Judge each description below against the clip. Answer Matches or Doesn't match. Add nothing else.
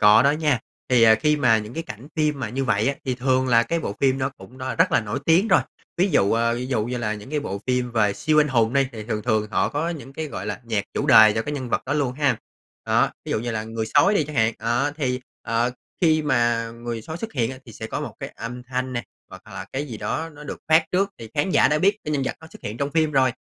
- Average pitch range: Matches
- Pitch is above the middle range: Doesn't match